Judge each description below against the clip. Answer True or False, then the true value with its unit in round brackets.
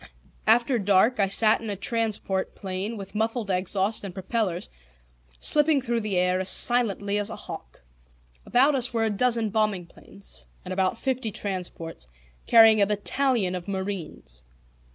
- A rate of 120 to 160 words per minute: True (155 wpm)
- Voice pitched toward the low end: False (205 Hz)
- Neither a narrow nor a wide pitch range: True (3.4 semitones)